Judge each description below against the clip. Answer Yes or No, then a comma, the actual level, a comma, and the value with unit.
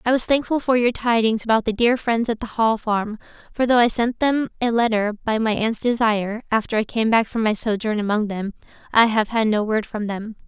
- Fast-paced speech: Yes, fast, 235 wpm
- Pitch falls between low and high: No, high, 225 Hz